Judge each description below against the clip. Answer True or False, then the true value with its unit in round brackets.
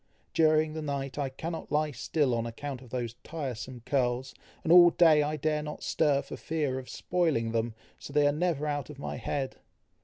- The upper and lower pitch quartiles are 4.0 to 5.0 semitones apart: False (3.1 semitones)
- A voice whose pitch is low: False (145 Hz)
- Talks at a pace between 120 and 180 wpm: False (195 wpm)